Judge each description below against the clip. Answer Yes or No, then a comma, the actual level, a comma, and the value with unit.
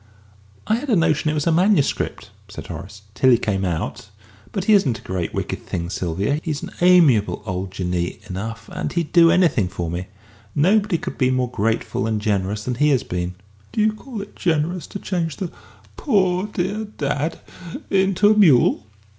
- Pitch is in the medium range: Yes, medium, 145 Hz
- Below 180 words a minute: No, average, 185 wpm